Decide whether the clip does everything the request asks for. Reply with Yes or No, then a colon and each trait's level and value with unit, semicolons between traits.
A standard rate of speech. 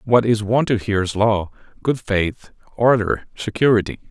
Yes: average, 145 wpm